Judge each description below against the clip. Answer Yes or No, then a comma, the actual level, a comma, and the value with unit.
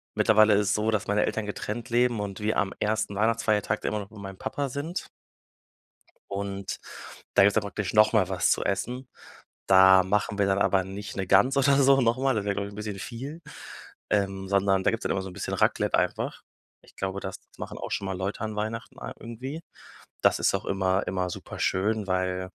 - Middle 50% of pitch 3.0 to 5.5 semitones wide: No, narrow, 2.5 semitones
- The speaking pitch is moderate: No, low, 105 Hz